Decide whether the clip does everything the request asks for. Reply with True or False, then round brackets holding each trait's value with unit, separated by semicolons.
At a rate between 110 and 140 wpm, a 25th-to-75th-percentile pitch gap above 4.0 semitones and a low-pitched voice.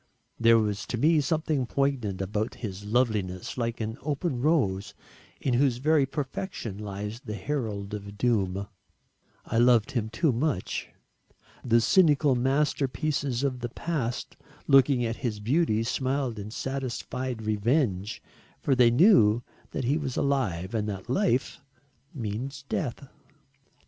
True (135 wpm; 4.5 semitones; 120 Hz)